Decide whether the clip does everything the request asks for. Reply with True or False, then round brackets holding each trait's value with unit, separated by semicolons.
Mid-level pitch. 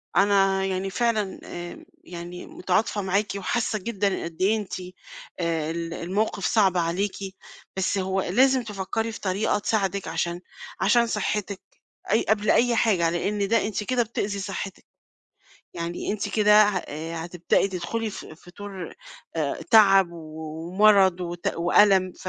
False (195 Hz)